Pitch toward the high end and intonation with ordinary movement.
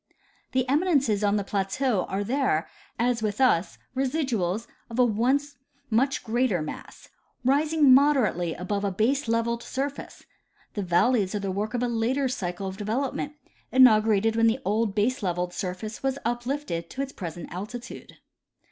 Yes: high, 230 Hz; average, 4.8 semitones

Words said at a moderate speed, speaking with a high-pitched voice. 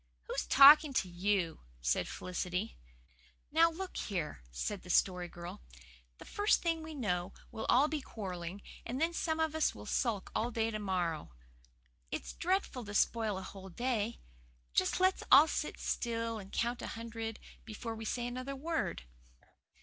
Yes: average, 165 wpm; high, 225 Hz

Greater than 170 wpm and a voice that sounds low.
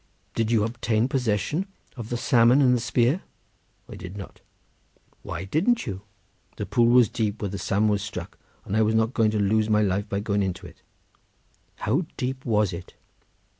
Yes: average, 185 wpm; low, 110 Hz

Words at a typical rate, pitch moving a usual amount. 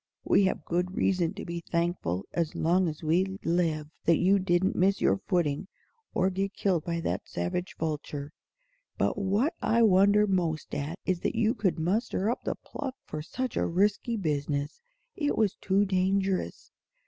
Yes: average, 170 wpm; average, 3.4 semitones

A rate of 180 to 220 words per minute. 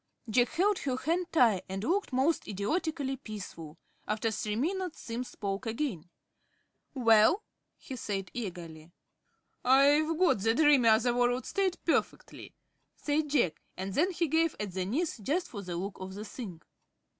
No: average, 155 wpm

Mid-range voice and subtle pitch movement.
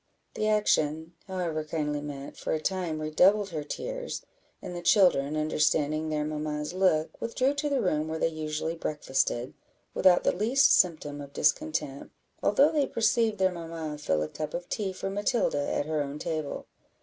No: medium, 160 Hz; average, 4.4 semitones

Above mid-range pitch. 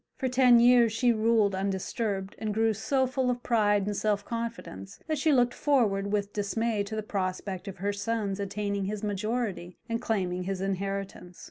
Yes: high, 210 Hz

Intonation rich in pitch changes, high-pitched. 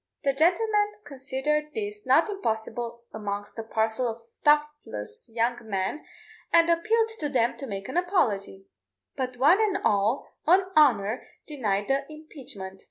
Yes: wide, 6.9 semitones; very high, 265 Hz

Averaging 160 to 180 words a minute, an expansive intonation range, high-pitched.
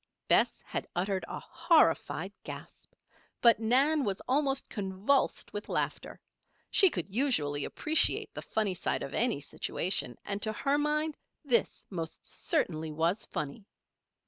No: slow, 135 wpm; wide, 7.8 semitones; high, 215 Hz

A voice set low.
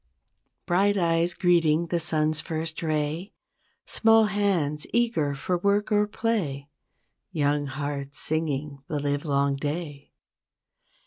No: medium, 155 Hz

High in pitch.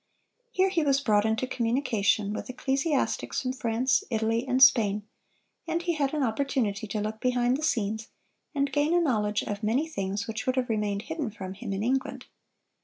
Yes: high, 240 Hz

